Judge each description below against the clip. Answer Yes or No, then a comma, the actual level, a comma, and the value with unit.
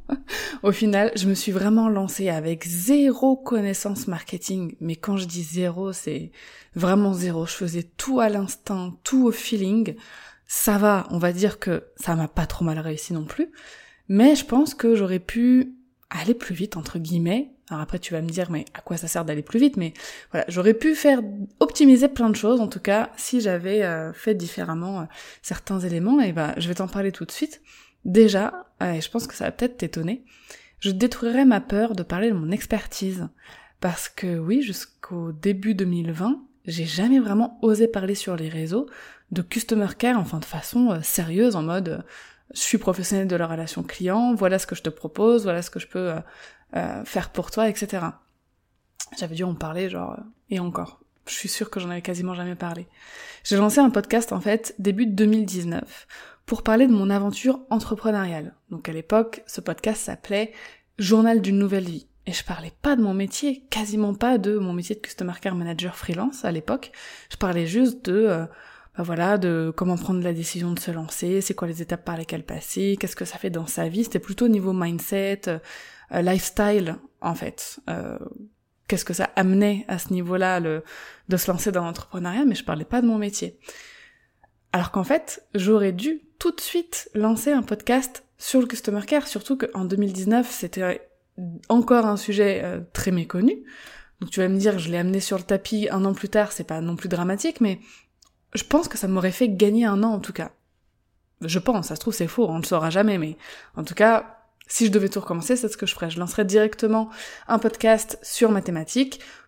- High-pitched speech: Yes, high, 200 Hz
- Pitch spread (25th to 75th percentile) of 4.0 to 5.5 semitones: Yes, average, 4.3 semitones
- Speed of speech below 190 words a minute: No, average, 200 wpm